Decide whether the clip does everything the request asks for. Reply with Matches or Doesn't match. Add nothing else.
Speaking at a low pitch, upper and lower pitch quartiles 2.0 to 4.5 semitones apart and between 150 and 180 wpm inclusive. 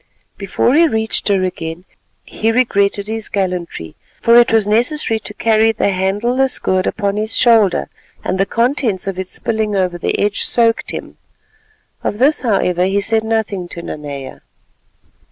Doesn't match